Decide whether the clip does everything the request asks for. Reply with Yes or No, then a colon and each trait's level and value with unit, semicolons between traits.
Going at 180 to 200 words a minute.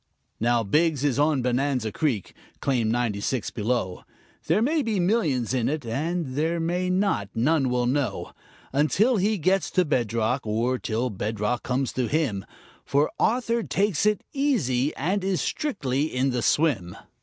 No: average, 155 wpm